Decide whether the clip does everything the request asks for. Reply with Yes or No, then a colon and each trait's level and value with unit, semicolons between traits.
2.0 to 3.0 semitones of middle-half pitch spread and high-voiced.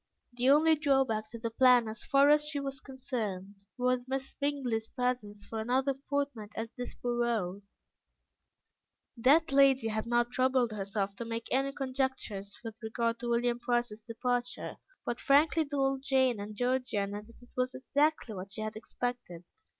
No: average, 3.4 semitones; high, 245 Hz